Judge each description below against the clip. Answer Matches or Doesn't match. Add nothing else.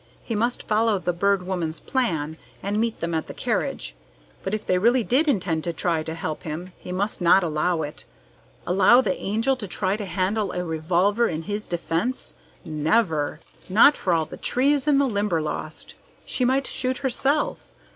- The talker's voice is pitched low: Doesn't match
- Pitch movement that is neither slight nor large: Doesn't match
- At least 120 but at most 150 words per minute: Doesn't match